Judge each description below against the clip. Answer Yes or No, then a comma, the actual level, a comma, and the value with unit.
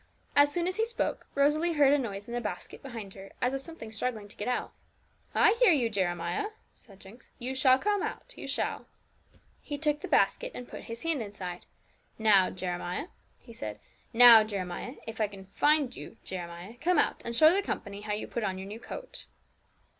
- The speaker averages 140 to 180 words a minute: No, average, 200 wpm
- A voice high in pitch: Yes, high, 235 Hz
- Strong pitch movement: Yes, wide, 6.6 semitones